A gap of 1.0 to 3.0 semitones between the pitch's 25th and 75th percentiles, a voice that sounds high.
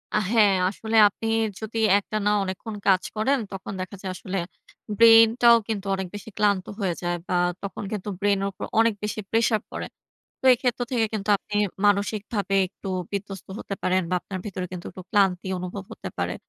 Yes: narrow, 2.4 semitones; high, 205 Hz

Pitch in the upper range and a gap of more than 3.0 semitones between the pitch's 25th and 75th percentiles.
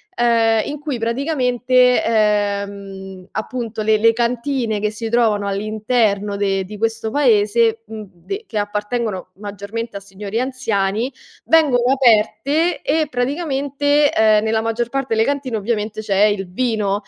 Yes: high, 225 Hz; average, 3.4 semitones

